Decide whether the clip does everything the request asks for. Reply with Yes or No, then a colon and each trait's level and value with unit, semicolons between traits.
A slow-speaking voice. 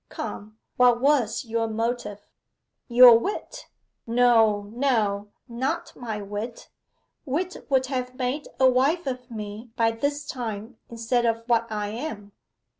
Yes: slow, 130 wpm